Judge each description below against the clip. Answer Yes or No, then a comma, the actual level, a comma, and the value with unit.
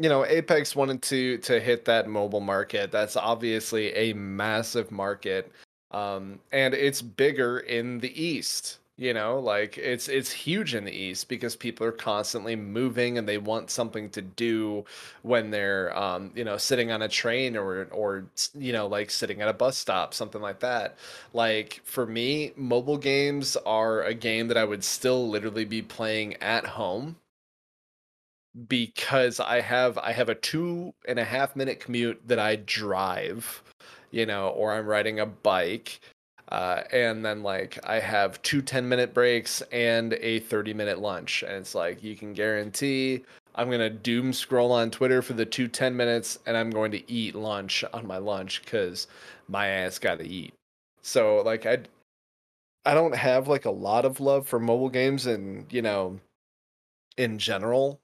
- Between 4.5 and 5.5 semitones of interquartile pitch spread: No, average, 3.2 semitones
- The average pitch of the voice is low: Yes, low, 115 Hz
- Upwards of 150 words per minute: Yes, average, 175 wpm